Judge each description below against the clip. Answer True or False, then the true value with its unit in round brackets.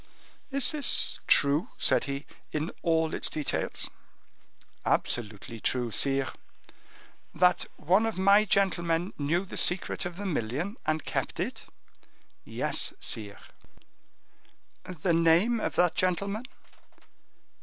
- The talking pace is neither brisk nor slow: False (110 wpm)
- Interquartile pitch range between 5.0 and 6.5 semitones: True (5.3 semitones)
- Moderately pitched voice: True (170 Hz)